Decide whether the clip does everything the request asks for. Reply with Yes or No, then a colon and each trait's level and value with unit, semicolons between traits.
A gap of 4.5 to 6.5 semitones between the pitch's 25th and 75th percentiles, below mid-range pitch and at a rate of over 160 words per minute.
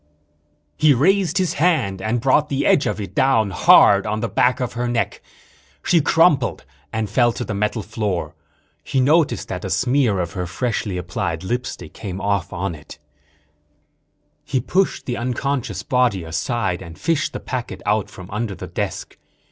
Yes: wide, 5.5 semitones; low, 115 Hz; average, 170 wpm